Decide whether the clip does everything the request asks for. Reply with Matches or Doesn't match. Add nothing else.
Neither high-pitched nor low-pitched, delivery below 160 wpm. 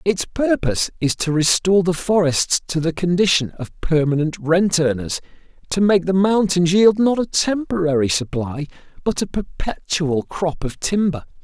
Matches